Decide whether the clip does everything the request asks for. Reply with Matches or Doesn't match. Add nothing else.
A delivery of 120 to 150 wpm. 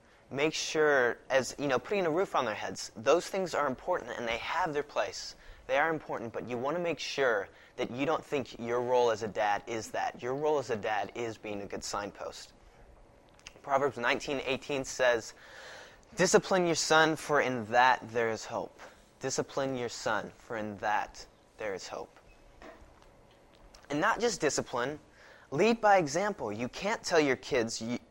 Doesn't match